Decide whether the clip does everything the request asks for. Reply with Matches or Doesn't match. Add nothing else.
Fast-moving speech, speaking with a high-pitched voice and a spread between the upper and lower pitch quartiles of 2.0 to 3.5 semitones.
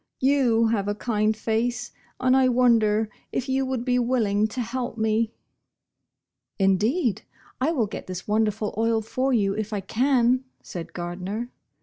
Doesn't match